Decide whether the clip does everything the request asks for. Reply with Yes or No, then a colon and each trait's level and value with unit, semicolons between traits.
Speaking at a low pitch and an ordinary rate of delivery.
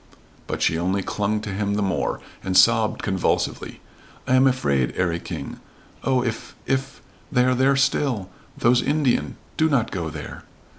Yes: low, 110 Hz; average, 160 wpm